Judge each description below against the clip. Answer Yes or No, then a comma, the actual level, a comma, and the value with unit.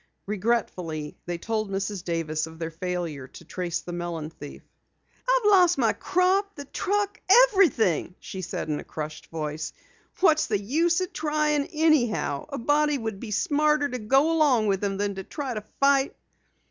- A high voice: Yes, high, 220 Hz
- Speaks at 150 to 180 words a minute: Yes, average, 165 wpm